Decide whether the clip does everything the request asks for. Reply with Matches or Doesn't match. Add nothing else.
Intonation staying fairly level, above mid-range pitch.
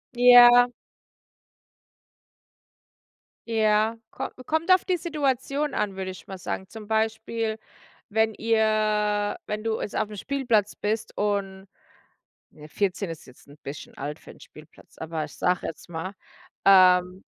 Doesn't match